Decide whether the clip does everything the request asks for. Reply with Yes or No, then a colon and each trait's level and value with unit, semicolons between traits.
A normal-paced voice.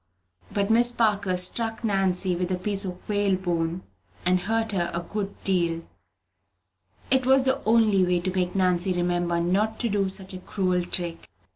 Yes: average, 170 wpm